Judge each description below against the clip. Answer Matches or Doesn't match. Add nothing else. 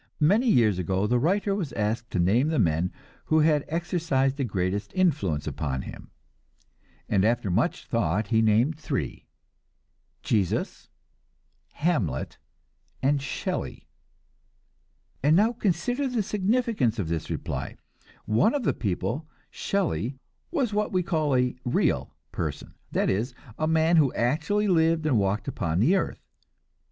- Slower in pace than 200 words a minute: Matches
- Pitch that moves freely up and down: Matches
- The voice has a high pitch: Doesn't match